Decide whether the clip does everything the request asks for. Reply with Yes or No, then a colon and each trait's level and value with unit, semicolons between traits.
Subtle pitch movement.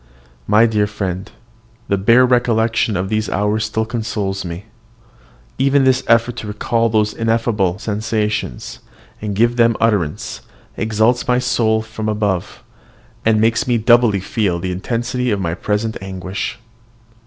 Yes: narrow, 2.3 semitones